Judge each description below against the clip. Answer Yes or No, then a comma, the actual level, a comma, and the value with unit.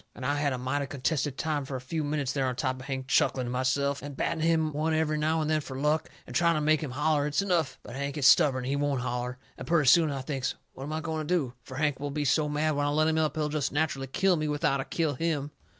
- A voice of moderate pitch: Yes, medium, 145 Hz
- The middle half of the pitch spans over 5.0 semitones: No, narrow, 2.6 semitones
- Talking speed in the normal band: No, fast, 290 wpm